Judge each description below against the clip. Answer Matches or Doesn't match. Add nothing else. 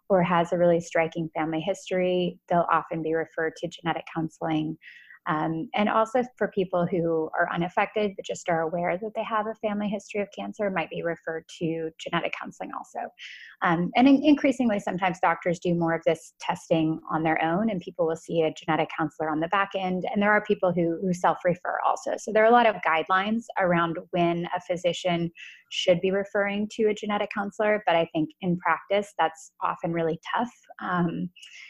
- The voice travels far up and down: Doesn't match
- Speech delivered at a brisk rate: Doesn't match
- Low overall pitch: Doesn't match